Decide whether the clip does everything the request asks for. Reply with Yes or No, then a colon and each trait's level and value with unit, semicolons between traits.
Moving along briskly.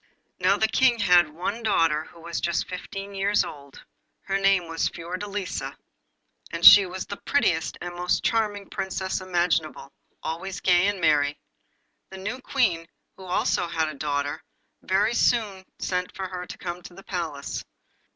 No: average, 160 wpm